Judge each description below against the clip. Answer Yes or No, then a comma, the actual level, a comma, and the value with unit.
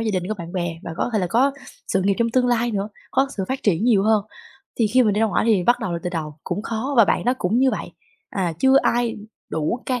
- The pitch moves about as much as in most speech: Yes, average, 4.7 semitones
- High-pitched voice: Yes, high, 215 Hz